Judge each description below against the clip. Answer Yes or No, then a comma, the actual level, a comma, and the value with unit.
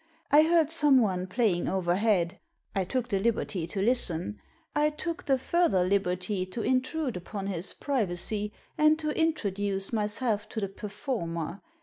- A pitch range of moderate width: No, wide, 6.0 semitones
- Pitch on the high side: Yes, high, 210 Hz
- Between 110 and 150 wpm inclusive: Yes, average, 140 wpm